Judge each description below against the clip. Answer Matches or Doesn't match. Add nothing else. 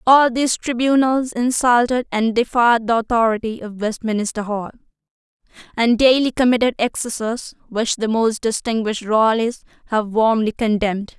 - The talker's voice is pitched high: Matches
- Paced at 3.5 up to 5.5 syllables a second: Matches